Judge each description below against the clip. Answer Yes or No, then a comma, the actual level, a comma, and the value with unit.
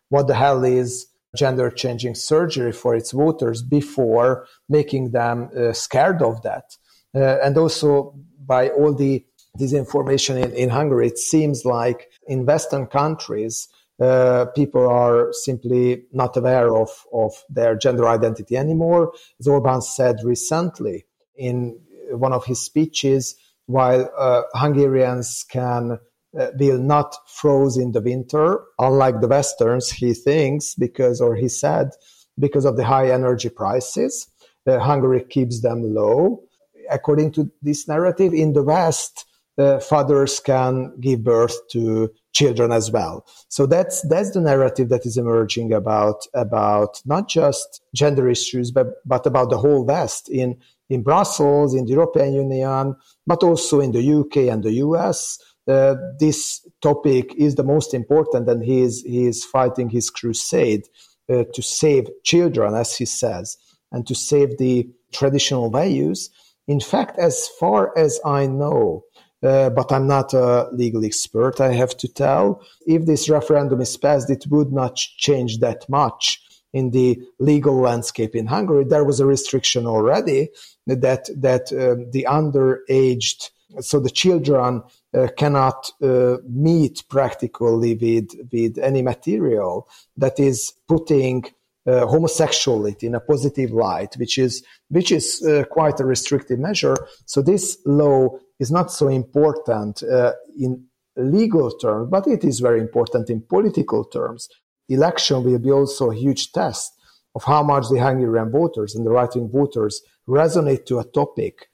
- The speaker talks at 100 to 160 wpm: Yes, average, 150 wpm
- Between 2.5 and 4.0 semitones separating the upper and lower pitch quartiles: Yes, average, 2.8 semitones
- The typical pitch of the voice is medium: No, low, 130 Hz